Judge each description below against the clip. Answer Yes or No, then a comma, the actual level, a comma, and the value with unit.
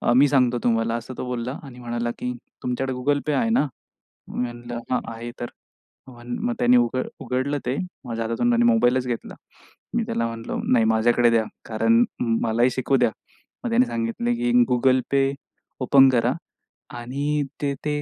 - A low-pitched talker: Yes, low, 125 Hz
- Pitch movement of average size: No, narrow, 2.2 semitones